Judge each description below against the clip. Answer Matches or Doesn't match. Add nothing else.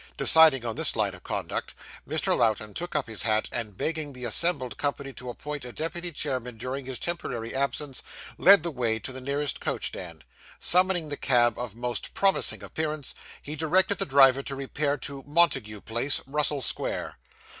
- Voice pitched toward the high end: Doesn't match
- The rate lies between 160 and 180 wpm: Matches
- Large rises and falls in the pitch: Doesn't match